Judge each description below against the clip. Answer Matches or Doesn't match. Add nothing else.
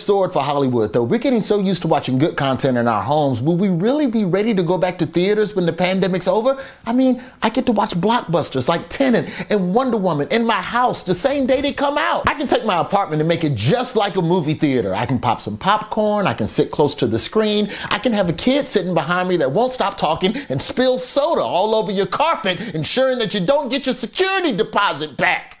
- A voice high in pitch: Matches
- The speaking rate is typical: Doesn't match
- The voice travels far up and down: Matches